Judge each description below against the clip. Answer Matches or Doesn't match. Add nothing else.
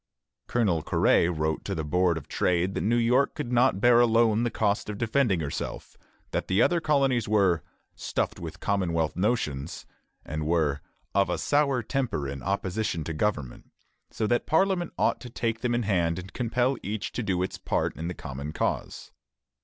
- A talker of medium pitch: Doesn't match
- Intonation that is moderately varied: Doesn't match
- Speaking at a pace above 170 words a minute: Matches